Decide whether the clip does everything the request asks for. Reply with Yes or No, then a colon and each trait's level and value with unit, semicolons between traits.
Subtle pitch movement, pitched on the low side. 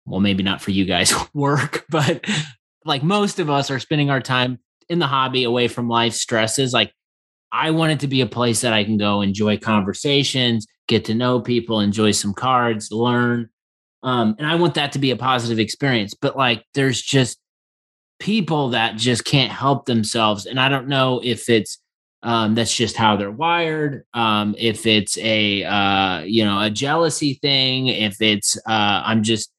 No: average, 4.1 semitones; low, 120 Hz